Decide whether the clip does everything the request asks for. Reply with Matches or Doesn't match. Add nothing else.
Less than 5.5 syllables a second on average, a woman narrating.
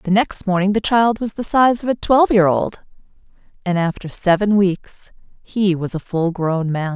Matches